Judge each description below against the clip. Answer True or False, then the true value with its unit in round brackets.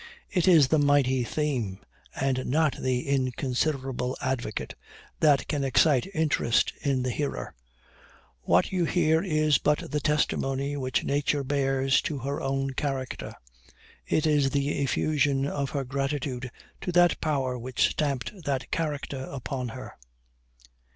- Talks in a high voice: False (140 Hz)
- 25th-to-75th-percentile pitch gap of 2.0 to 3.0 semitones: True (2.4 semitones)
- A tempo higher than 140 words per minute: False (135 wpm)